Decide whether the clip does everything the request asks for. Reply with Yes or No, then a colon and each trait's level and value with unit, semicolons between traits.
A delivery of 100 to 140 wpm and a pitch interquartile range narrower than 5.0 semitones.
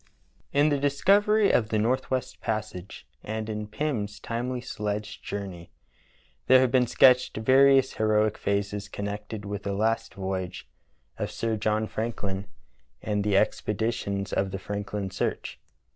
Yes: slow, 135 wpm; average, 3.5 semitones